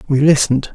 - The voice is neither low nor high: Yes, medium, 145 Hz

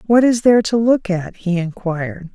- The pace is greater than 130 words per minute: Yes, fast, 205 wpm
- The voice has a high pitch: Yes, high, 200 Hz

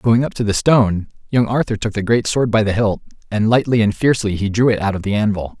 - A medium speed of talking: No, fast, 270 wpm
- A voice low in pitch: Yes, low, 110 Hz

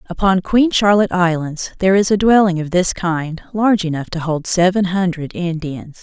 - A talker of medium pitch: Yes, medium, 180 Hz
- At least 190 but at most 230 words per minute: No, average, 180 wpm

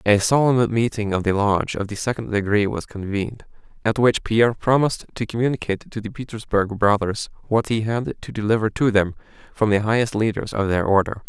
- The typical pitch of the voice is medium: No, low, 110 Hz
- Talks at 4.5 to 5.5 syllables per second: No, 5.8 syllables/s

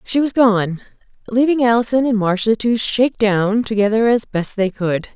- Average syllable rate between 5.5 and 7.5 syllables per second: No, 4.9 syllables/s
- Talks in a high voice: Yes, high, 220 Hz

